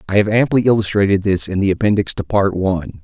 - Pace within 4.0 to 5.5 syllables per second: No, 6.3 syllables/s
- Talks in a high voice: No, low, 100 Hz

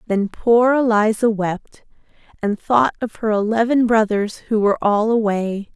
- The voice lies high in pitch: Yes, high, 220 Hz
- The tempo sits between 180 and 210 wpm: No, average, 145 wpm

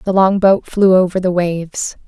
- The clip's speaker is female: Yes, female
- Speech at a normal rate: Yes, average, 175 wpm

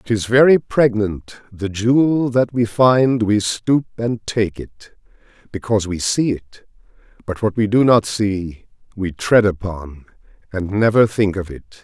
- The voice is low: Yes, low, 110 Hz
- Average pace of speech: Yes, average, 155 wpm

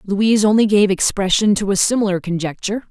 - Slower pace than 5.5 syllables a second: No, 6.3 syllables/s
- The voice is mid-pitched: No, high, 200 Hz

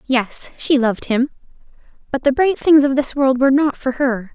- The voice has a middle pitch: No, very high, 270 Hz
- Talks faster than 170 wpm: Yes, fast, 205 wpm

